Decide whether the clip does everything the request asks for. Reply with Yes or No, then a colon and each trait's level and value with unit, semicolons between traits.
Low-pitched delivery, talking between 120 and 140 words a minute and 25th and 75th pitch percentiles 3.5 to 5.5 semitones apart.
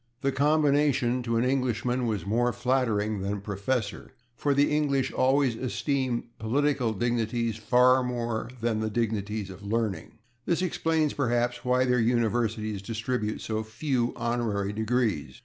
No: low, 120 Hz; slow, 135 wpm; average, 2.9 semitones